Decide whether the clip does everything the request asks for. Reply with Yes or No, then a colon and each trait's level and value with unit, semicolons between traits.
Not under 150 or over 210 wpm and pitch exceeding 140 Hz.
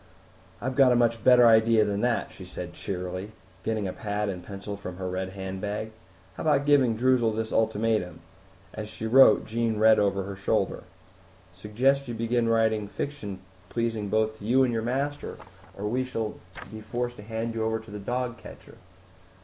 No: average, 180 wpm; low, 110 Hz